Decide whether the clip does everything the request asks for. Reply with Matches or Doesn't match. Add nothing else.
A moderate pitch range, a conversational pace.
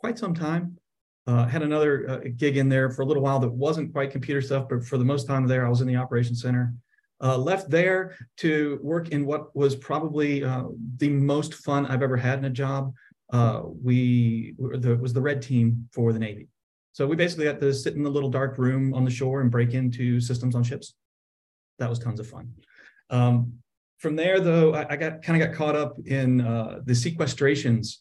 Doesn't match